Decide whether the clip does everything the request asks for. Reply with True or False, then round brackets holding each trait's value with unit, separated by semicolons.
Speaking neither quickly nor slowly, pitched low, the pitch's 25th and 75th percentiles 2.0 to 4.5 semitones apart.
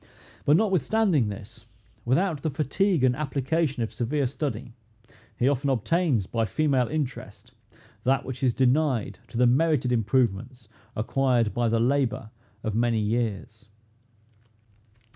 False (125 wpm; 130 Hz; 4.1 semitones)